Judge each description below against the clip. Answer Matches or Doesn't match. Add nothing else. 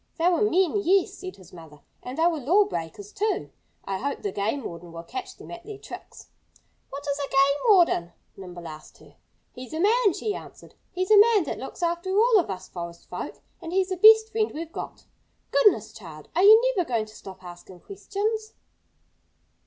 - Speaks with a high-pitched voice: Matches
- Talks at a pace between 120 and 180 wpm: Doesn't match